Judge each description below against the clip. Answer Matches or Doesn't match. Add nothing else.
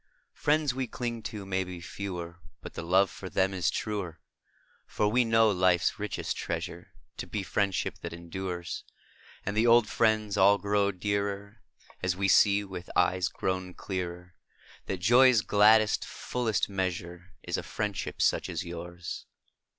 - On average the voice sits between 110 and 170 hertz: Doesn't match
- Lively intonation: Doesn't match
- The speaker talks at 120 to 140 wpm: Doesn't match